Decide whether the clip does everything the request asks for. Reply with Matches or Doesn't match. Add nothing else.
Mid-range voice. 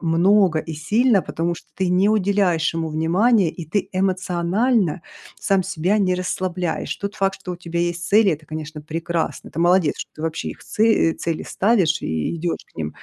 Matches